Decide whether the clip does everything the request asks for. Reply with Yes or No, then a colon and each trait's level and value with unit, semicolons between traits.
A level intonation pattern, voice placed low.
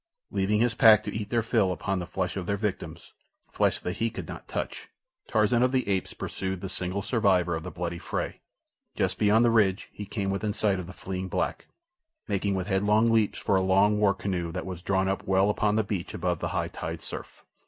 Yes: narrow, 2.3 semitones; low, 100 Hz